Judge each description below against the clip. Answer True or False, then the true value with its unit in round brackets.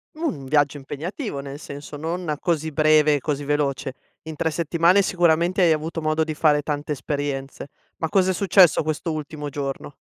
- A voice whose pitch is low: False (155 Hz)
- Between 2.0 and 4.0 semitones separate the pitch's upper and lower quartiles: True (2.5 semitones)